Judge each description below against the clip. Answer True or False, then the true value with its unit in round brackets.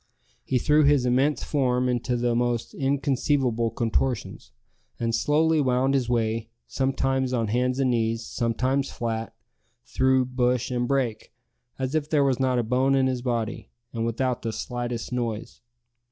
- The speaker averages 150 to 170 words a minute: True (155 wpm)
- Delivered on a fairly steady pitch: True (2.2 semitones)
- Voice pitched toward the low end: True (125 Hz)